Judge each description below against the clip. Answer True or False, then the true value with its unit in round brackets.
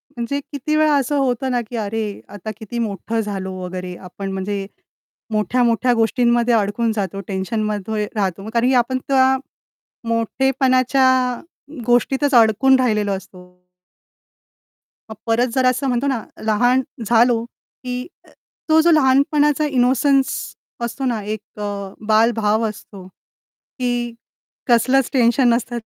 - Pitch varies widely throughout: False (3.5 semitones)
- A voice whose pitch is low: False (235 Hz)